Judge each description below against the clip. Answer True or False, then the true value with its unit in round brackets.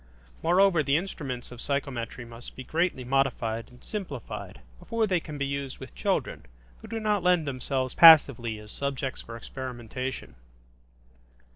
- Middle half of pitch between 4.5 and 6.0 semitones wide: True (5.0 semitones)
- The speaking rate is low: False (145 wpm)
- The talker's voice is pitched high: False (135 Hz)